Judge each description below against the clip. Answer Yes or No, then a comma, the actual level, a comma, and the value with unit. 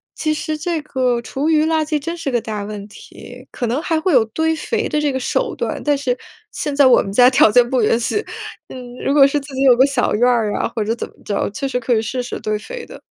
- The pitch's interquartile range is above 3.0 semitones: Yes, average, 4.2 semitones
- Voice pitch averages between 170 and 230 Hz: No, very high, 260 Hz